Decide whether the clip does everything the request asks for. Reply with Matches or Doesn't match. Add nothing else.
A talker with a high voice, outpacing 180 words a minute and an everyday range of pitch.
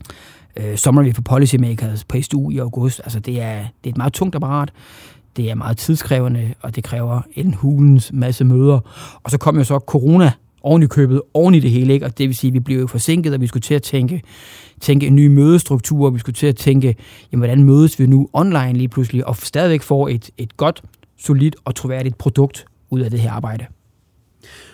Doesn't match